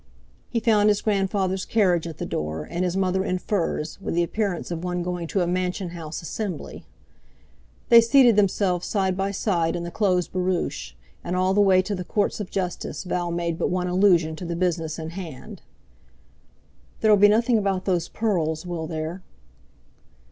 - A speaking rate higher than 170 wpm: Yes, average, 180 wpm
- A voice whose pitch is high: No, medium, 180 Hz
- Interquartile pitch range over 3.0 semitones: No, average, 2.7 semitones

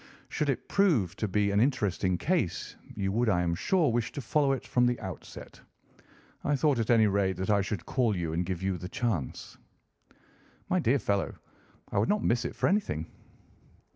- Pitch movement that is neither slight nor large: No, wide, 6.0 semitones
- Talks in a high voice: No, low, 105 Hz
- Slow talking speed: No, average, 195 wpm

